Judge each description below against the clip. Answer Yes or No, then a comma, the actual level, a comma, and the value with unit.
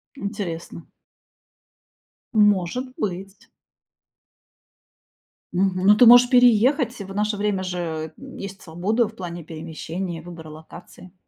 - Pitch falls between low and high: No, high, 195 Hz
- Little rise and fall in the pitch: No, average, 3.9 semitones